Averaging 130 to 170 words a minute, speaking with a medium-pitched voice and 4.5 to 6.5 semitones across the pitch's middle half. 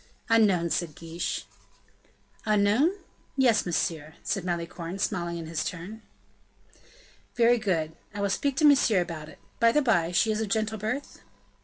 No: average, 155 wpm; high, 195 Hz; average, 4.8 semitones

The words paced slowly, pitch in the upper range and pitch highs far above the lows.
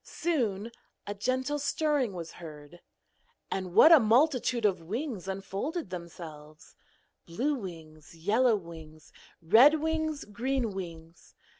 Yes: slow, 115 wpm; high, 205 Hz; wide, 8.0 semitones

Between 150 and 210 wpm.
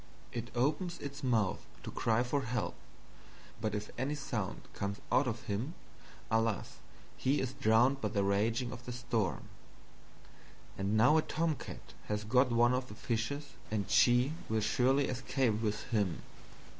Yes: average, 155 wpm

